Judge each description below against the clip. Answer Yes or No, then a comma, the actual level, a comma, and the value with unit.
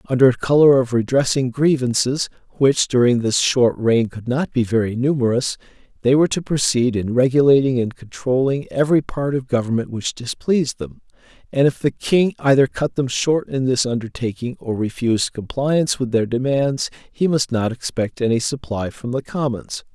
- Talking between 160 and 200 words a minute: Yes, average, 170 wpm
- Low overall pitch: Yes, low, 130 Hz